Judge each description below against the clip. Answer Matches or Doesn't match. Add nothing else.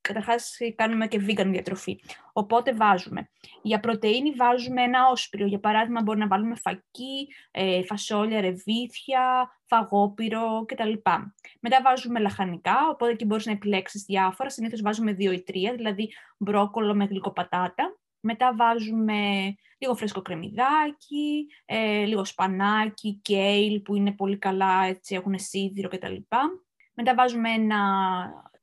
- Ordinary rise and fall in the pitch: Matches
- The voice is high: Matches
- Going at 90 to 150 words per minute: Matches